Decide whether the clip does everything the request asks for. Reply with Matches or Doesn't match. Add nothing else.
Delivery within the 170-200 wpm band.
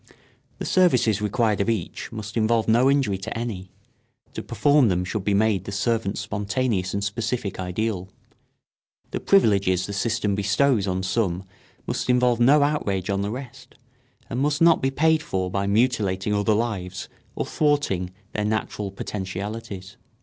Doesn't match